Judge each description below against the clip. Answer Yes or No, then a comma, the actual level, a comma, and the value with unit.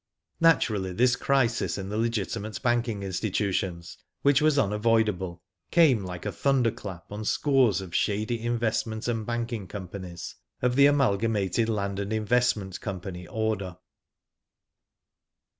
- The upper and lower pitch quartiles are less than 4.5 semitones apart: Yes, average, 3.6 semitones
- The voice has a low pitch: Yes, low, 110 Hz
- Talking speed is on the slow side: Yes, slow, 120 wpm